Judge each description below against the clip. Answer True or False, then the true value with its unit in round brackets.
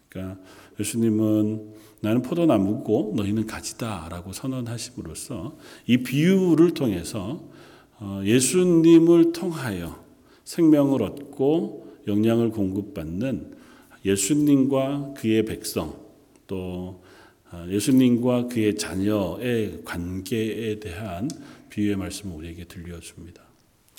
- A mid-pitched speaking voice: False (110 Hz)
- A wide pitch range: False (4.8 semitones)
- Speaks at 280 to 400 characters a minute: False (235 characters per minute)